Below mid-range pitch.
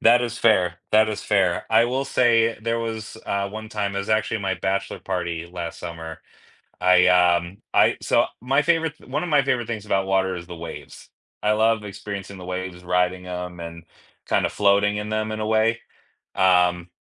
Yes: low, 100 Hz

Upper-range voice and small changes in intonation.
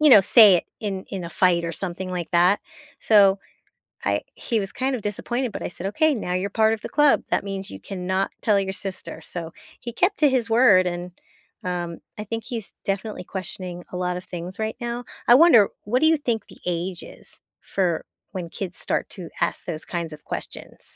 No: high, 195 Hz; average, 4.0 semitones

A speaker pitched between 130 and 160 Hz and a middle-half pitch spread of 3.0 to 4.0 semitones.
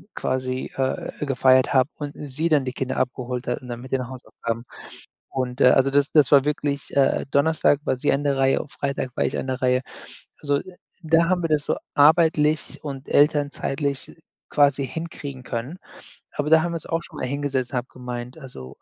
No: medium, 140 Hz; narrow, 2.5 semitones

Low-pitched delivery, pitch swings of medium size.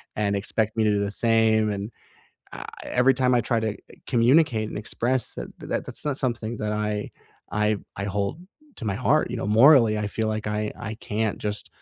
No: low, 110 Hz; narrow, 2.2 semitones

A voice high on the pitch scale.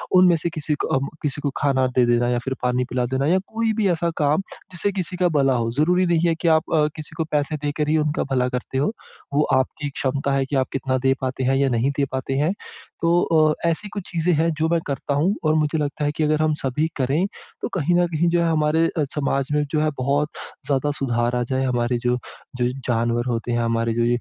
No: medium, 145 Hz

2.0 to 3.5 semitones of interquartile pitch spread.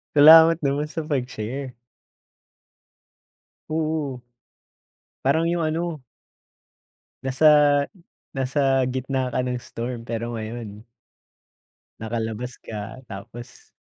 No: average, 3.9 semitones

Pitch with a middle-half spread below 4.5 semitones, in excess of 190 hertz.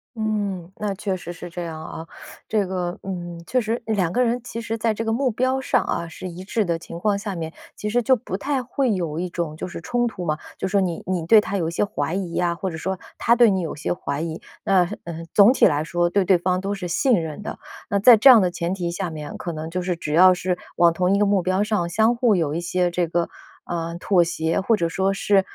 No: average, 3.7 semitones; medium, 185 Hz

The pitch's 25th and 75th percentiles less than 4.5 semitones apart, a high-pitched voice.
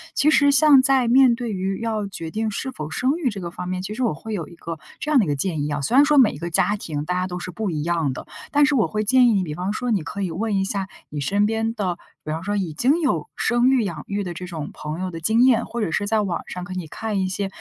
No: wide, 5.4 semitones; high, 200 Hz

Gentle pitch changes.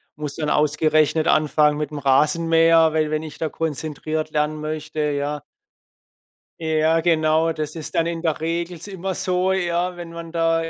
Yes: narrow, 1.5 semitones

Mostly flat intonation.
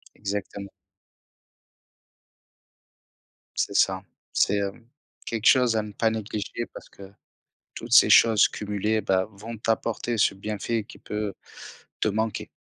Yes: narrow, 2.0 semitones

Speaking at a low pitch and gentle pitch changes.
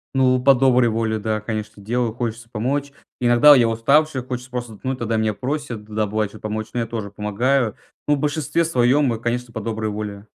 No: low, 120 Hz; average, 3.0 semitones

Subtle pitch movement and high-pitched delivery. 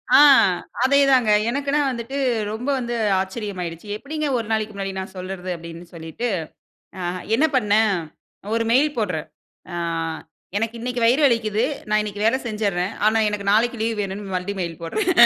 No: average, 3.8 semitones; high, 215 Hz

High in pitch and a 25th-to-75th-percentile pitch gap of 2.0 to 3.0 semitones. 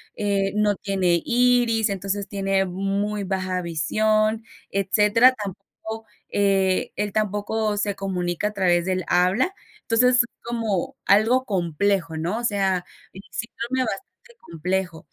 Yes: high, 200 Hz; average, 2.7 semitones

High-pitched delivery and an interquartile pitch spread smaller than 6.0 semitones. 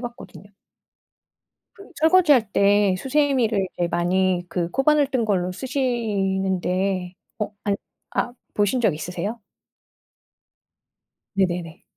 Yes: high, 200 Hz; average, 5.2 semitones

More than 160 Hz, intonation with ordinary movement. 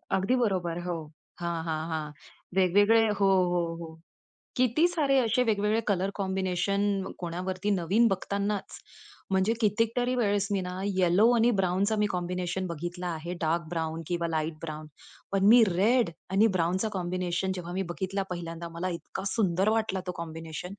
Yes: medium, 185 Hz; average, 3.0 semitones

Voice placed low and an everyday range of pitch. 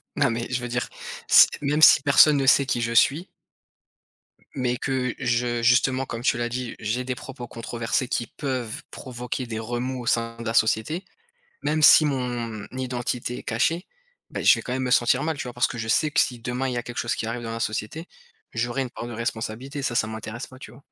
No: low, 125 Hz; narrow, 2.1 semitones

